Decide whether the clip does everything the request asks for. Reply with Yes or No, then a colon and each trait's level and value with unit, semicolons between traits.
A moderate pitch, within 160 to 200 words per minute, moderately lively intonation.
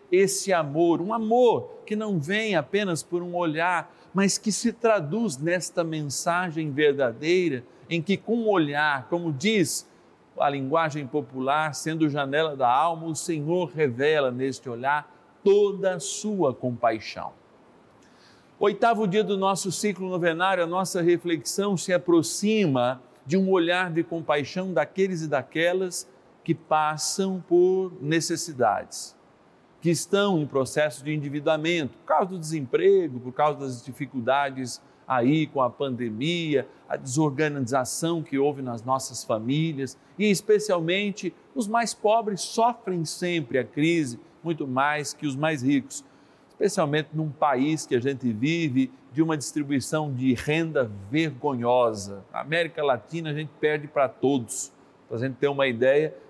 No: medium, 160 Hz; average, 140 wpm; average, 4.6 semitones